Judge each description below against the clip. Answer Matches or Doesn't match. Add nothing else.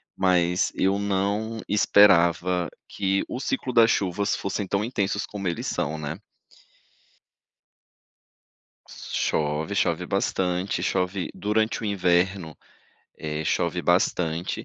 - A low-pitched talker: Matches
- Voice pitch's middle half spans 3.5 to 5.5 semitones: Doesn't match